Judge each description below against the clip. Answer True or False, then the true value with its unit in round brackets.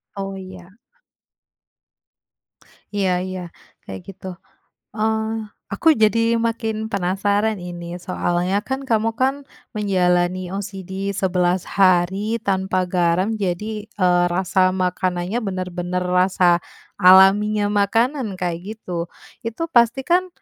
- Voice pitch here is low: False (190 Hz)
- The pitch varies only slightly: False (3.2 semitones)